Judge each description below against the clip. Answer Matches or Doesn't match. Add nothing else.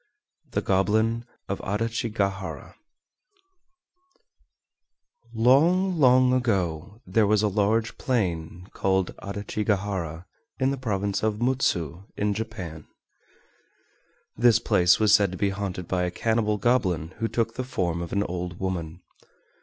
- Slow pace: Matches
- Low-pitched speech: Matches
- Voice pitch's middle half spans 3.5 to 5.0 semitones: Matches